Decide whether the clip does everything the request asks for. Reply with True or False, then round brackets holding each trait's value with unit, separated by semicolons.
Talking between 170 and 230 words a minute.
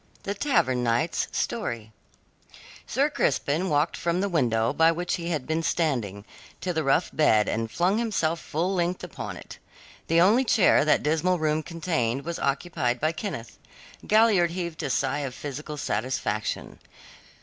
False (155 wpm)